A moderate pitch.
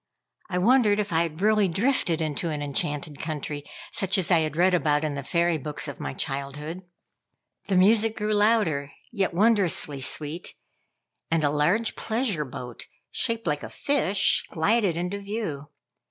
Yes: medium, 170 Hz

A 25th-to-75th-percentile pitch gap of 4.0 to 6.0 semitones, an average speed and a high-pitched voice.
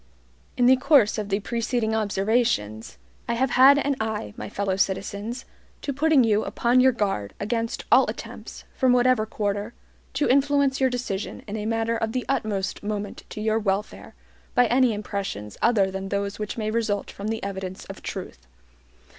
No: average, 3.6 semitones; average, 170 wpm; high, 220 Hz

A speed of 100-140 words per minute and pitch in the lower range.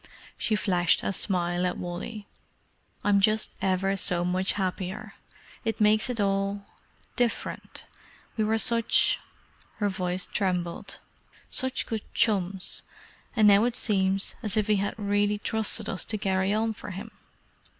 No: slow, 135 wpm; high, 200 Hz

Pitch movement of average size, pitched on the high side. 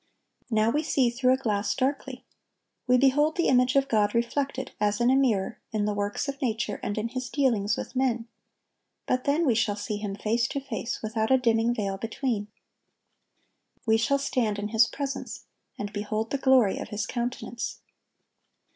Yes: average, 3.6 semitones; high, 235 Hz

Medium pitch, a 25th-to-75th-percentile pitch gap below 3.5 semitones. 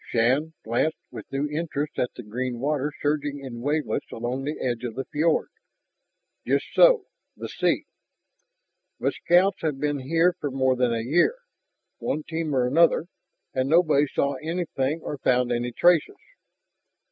No: medium, 145 Hz; average, 3.9 semitones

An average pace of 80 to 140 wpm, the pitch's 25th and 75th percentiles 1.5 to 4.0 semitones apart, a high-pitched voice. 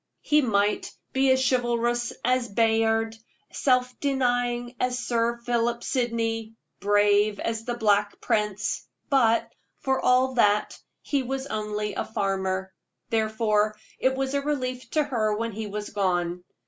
Yes: slow, 135 wpm; average, 3.1 semitones; high, 230 Hz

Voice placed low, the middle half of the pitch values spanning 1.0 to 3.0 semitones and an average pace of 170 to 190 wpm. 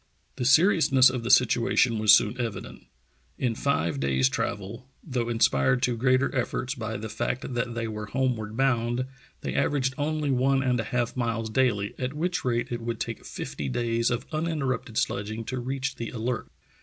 Yes: low, 120 Hz; average, 2.7 semitones; average, 175 wpm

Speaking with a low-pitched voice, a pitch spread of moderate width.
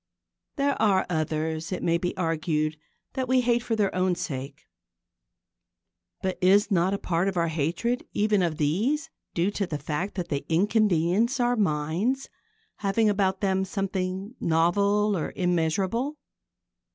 No: high, 190 Hz; average, 4.3 semitones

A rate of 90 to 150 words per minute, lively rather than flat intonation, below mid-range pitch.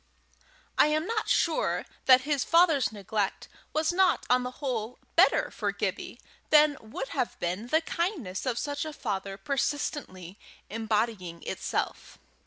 No: average, 140 wpm; wide, 6.3 semitones; very high, 255 Hz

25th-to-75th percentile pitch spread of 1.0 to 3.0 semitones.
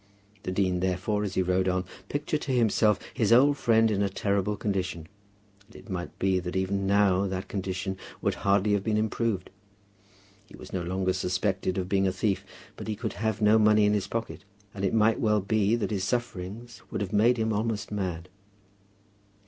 Yes: average, 2.7 semitones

